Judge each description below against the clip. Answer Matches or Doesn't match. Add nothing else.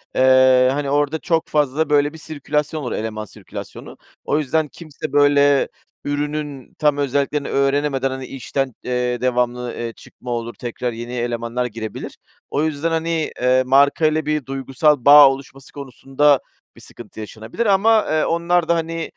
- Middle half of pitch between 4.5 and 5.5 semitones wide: Doesn't match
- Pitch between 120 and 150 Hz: Matches